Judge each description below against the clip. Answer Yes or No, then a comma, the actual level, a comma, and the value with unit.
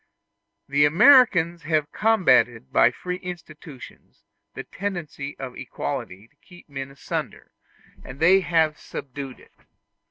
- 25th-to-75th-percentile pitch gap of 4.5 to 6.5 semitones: Yes, average, 4.8 semitones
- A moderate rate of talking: No, slow, 120 wpm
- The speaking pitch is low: No, medium, 155 Hz